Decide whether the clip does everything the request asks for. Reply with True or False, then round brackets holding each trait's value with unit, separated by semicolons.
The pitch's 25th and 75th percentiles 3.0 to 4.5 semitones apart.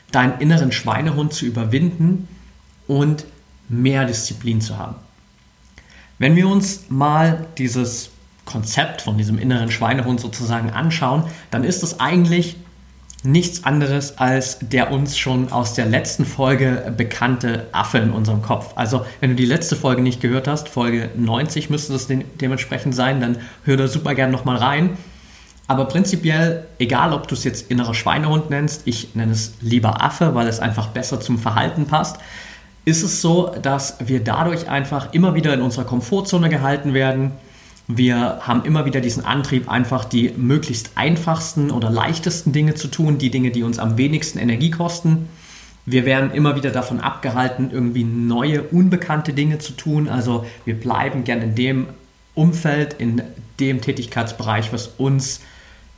True (4.0 semitones)